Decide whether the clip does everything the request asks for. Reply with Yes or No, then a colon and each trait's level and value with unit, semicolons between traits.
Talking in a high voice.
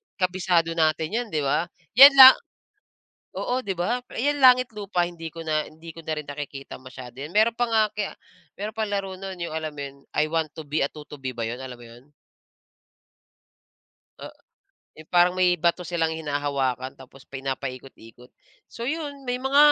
No: medium, 165 Hz